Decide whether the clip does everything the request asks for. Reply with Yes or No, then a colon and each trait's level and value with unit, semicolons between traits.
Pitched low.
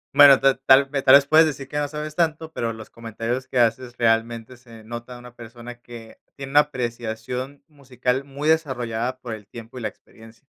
Yes: low, 125 Hz